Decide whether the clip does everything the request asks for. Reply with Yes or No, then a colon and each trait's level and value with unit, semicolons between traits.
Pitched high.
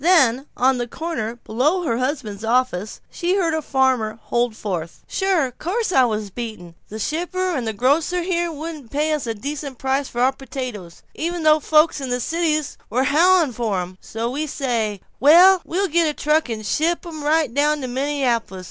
Yes: very high, 275 Hz